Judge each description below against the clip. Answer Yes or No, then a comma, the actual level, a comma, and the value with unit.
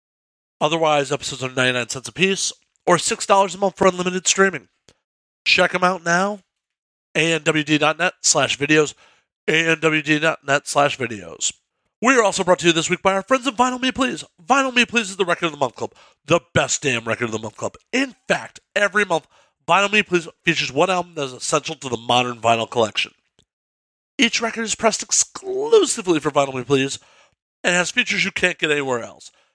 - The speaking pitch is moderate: Yes, medium, 170 Hz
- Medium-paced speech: Yes, average, 185 wpm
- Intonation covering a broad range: Yes, wide, 5.9 semitones